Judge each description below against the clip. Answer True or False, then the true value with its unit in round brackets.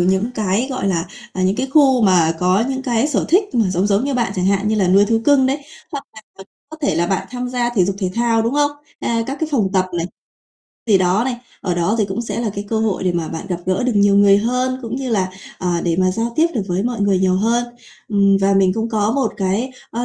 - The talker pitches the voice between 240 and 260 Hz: False (210 Hz)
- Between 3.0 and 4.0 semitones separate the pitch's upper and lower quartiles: False (4.5 semitones)